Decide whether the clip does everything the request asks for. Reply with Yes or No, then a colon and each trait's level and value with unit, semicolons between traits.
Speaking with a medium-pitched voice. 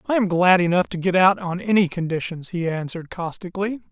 Yes: medium, 180 Hz